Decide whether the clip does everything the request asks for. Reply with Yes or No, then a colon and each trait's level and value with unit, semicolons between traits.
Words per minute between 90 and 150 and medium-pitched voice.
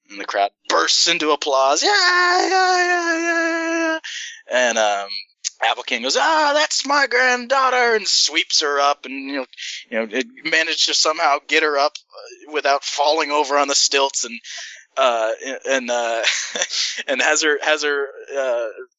No: average, 160 wpm; medium, 155 Hz